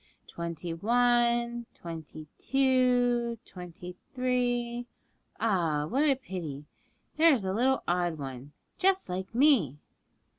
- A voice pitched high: Yes, high, 235 Hz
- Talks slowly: Yes, slow, 110 wpm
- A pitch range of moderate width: No, wide, 6.6 semitones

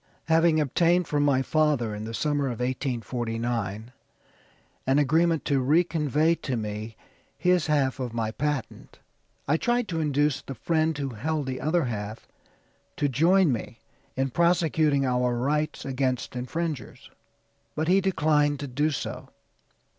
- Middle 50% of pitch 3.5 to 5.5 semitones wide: Yes, average, 4.1 semitones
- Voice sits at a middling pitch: Yes, medium, 145 Hz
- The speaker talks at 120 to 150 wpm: Yes, average, 145 wpm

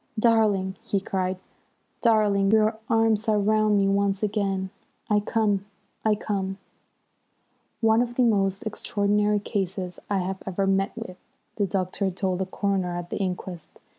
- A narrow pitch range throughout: Yes, narrow, 2.1 semitones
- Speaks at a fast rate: No, average, 145 wpm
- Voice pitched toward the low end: No, high, 200 Hz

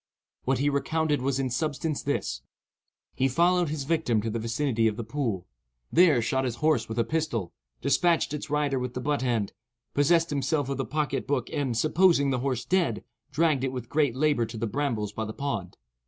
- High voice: No, low, 135 Hz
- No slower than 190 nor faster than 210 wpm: Yes, average, 195 wpm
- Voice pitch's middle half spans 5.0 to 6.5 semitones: No, average, 4.3 semitones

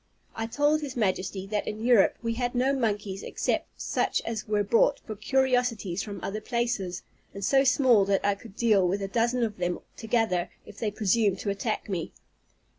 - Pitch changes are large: No, average, 3.3 semitones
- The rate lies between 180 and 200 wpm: Yes, average, 190 wpm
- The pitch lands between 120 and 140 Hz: No, high, 215 Hz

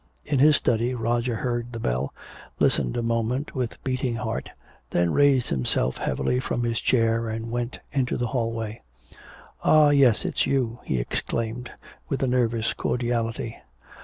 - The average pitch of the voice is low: Yes, low, 120 Hz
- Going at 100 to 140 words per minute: No, average, 150 wpm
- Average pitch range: No, narrow, 2.0 semitones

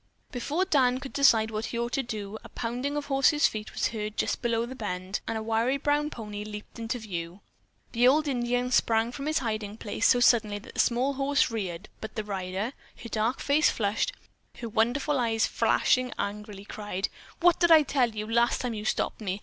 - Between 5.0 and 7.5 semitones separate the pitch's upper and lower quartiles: No, average, 3.7 semitones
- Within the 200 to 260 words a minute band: Yes, fast, 205 wpm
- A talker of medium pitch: No, high, 230 Hz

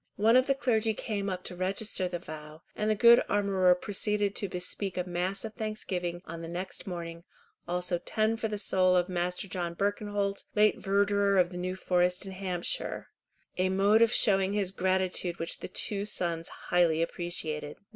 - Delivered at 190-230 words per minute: No, average, 175 wpm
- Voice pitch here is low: No, medium, 185 Hz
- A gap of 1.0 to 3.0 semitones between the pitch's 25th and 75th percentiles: Yes, narrow, 2.6 semitones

